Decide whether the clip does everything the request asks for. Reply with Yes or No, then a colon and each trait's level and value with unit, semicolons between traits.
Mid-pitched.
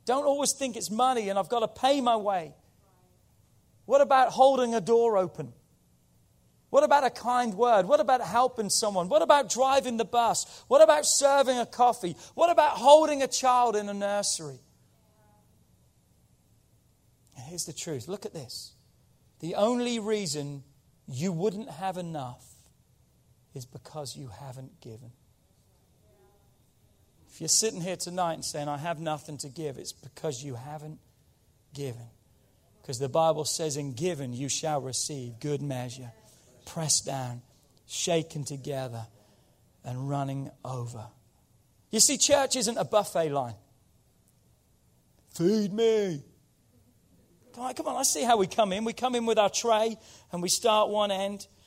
Yes: medium, 170 Hz